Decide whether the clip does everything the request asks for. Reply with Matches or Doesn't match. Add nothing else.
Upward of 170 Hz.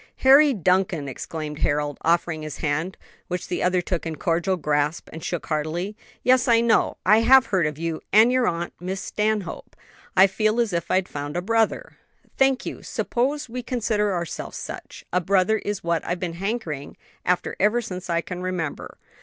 Matches